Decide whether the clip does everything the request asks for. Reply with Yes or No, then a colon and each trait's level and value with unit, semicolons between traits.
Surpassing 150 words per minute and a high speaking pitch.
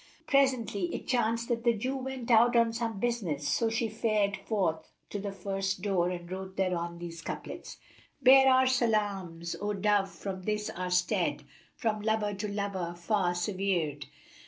Yes: average, 165 wpm; high, 205 Hz